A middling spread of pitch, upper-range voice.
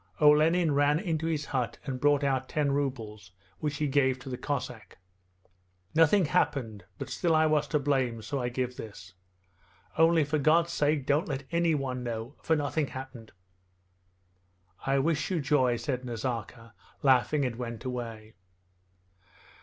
No: average, 3.6 semitones; medium, 140 Hz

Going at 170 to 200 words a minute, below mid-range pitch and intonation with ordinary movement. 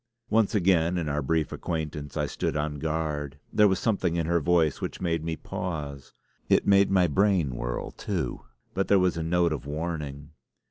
Yes: average, 185 wpm; very low, 80 Hz; average, 3.6 semitones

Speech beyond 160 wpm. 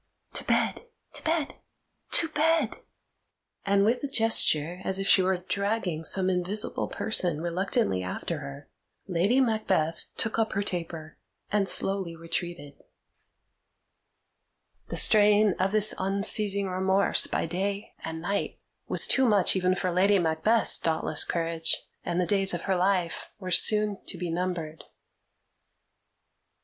No: slow, 135 wpm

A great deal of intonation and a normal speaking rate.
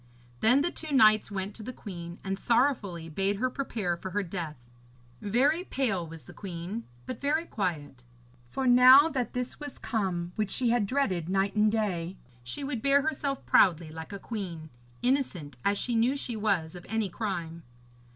Yes: wide, 6.5 semitones; average, 180 wpm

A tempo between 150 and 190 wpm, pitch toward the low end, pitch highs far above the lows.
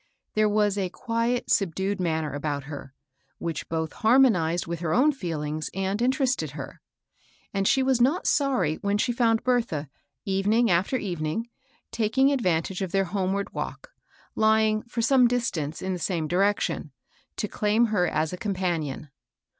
No: average, 155 wpm; high, 195 Hz; wide, 5.9 semitones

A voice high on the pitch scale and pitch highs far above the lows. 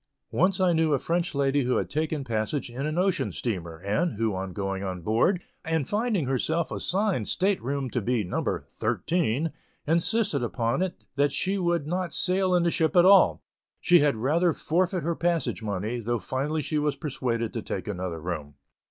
No: medium, 145 Hz; wide, 7.3 semitones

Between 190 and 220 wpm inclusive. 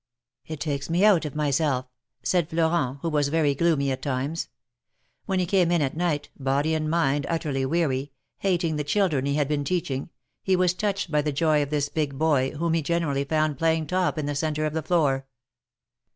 Yes: average, 200 wpm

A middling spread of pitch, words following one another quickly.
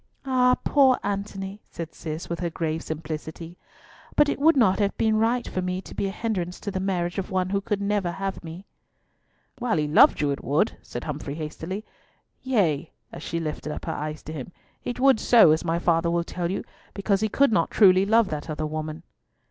Yes: average, 4.5 semitones; fast, 210 wpm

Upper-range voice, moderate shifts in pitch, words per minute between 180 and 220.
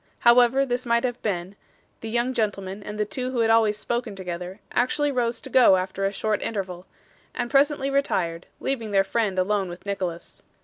Yes: high, 215 Hz; average, 4.1 semitones; average, 185 wpm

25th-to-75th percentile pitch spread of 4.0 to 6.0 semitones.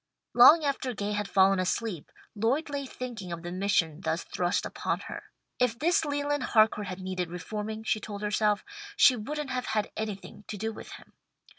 Yes: average, 4.8 semitones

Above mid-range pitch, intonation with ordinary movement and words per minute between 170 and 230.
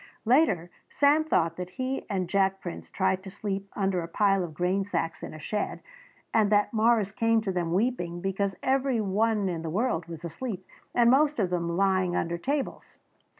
Yes: high, 195 Hz; average, 4.3 semitones; average, 190 wpm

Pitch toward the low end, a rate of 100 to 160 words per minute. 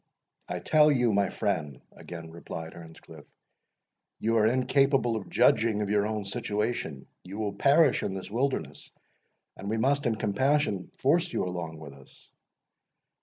Yes: low, 105 Hz; average, 150 wpm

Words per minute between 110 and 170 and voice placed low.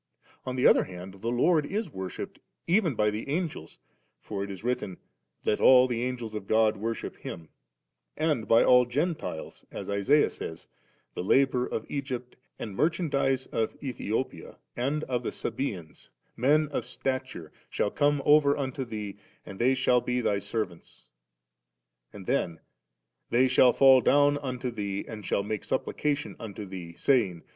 Yes: average, 160 wpm; low, 120 Hz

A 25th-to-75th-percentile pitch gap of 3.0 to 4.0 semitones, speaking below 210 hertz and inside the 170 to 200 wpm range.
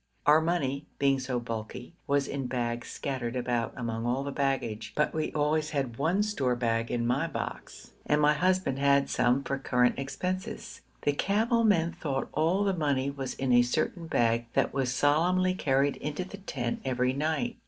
No: average, 4.5 semitones; medium, 140 Hz; average, 180 wpm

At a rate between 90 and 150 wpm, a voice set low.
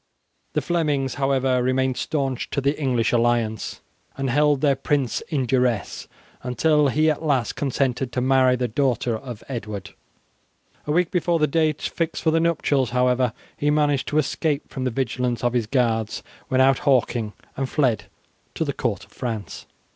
No: average, 170 wpm; low, 130 Hz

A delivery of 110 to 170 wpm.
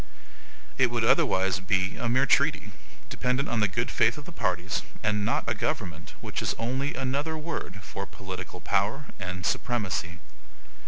Yes: average, 160 wpm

